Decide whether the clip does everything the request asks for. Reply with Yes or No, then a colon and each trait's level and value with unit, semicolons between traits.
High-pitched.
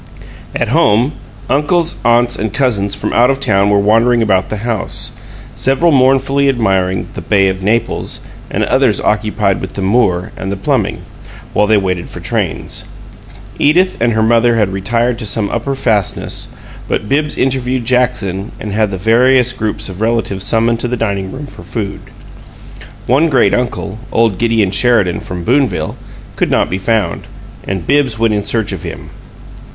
No: low, 115 Hz